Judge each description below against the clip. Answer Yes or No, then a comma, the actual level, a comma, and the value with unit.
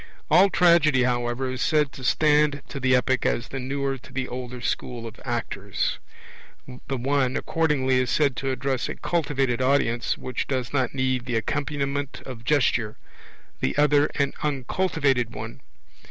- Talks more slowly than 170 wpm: Yes, average, 155 wpm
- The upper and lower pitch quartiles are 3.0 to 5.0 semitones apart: No, narrow, 2.4 semitones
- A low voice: Yes, low, 130 Hz